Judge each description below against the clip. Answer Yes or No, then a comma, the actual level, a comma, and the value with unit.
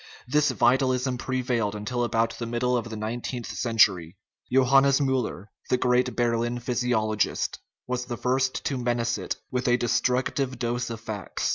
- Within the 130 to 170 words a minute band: Yes, average, 150 wpm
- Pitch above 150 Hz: No, low, 120 Hz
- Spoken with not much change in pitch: Yes, narrow, 1.6 semitones